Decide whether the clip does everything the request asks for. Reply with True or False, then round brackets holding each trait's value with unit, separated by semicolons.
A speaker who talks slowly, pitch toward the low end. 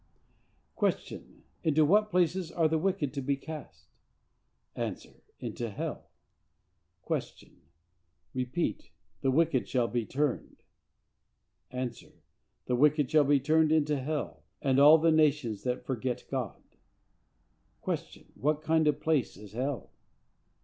False (120 wpm; 145 Hz)